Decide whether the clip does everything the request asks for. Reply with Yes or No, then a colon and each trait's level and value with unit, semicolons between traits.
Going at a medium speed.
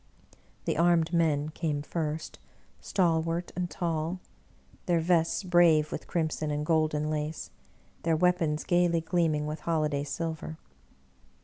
No: slow, 120 wpm